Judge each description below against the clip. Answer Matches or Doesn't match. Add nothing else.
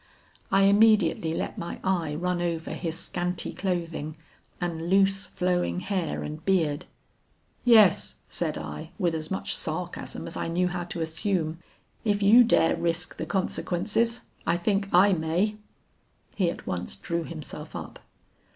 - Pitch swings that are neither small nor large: Matches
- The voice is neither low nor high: Matches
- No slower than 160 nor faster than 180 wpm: Doesn't match